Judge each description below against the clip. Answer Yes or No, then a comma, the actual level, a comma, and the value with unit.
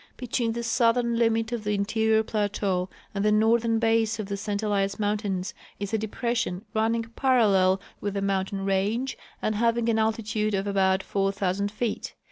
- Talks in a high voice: Yes, high, 215 Hz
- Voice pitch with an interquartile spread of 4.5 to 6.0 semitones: No, narrow, 2.4 semitones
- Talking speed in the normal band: Yes, average, 165 wpm